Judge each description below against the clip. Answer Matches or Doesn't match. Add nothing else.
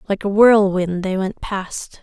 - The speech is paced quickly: Doesn't match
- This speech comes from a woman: Matches